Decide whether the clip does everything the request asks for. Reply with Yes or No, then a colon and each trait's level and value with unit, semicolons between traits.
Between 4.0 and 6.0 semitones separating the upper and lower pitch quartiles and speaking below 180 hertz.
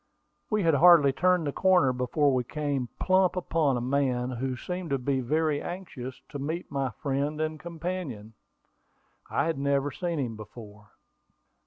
Yes: average, 4.6 semitones; medium, 140 Hz